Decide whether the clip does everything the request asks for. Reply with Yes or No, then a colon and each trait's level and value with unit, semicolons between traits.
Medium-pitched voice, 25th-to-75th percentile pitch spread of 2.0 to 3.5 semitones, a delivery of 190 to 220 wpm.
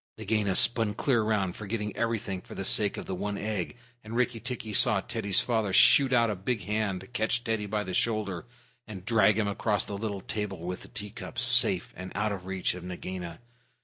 No: low, 105 Hz; average, 2.9 semitones; average, 200 wpm